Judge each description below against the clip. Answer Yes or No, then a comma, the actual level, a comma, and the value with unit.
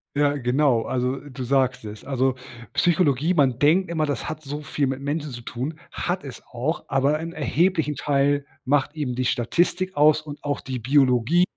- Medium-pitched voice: Yes, medium, 145 Hz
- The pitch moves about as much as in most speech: Yes, average, 3.0 semitones